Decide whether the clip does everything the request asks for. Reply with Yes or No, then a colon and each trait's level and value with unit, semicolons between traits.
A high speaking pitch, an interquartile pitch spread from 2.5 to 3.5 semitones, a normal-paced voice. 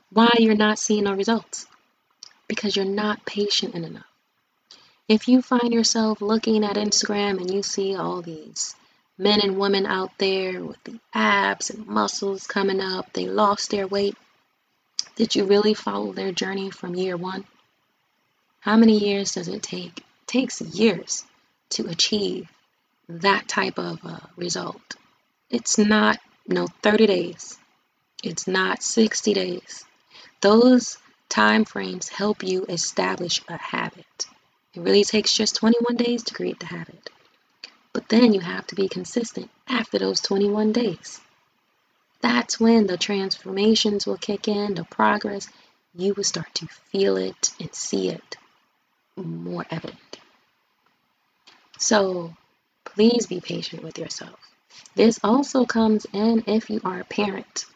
Yes: high, 205 Hz; average, 3.0 semitones; average, 145 wpm